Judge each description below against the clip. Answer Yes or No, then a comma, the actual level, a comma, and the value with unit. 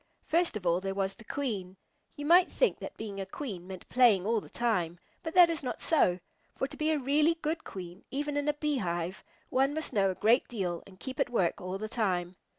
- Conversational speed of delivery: No, fast, 230 wpm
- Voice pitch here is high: Yes, high, 225 Hz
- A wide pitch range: Yes, wide, 7.6 semitones